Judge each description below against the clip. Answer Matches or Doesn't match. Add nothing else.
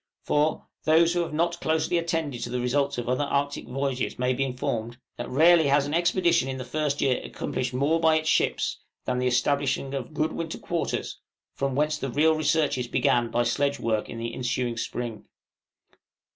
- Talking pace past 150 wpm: Matches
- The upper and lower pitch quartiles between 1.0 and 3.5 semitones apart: Doesn't match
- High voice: Doesn't match